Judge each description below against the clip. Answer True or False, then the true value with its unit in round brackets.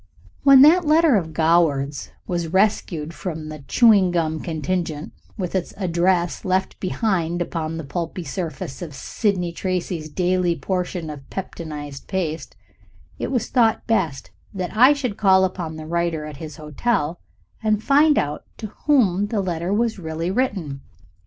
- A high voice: False (175 Hz)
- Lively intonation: False (4.1 semitones)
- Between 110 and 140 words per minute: False (150 wpm)